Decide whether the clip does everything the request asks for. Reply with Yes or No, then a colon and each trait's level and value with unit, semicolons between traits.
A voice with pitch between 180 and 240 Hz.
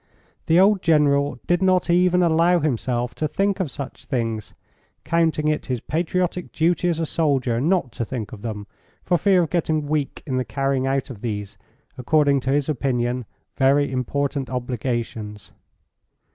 No: medium, 140 Hz